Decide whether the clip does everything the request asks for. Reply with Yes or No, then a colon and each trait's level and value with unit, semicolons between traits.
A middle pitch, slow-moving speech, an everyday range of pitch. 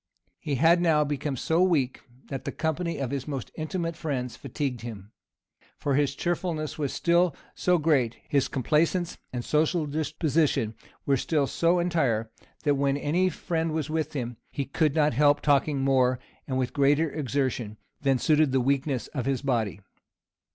No: medium, 145 Hz; average, 165 wpm; average, 3.4 semitones